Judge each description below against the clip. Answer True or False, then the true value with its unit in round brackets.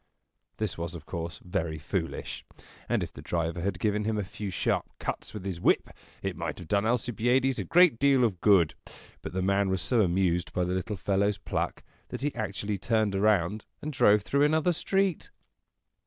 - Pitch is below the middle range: True (100 Hz)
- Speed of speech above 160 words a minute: True (190 wpm)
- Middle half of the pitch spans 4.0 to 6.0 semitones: True (4.5 semitones)